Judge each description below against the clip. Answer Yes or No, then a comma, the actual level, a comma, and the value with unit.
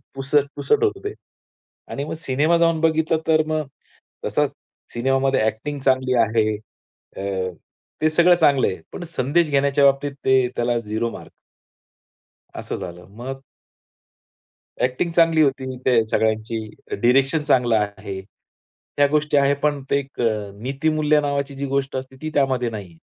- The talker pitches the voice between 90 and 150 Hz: Yes, low, 135 Hz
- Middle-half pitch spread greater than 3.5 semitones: Yes, average, 4.1 semitones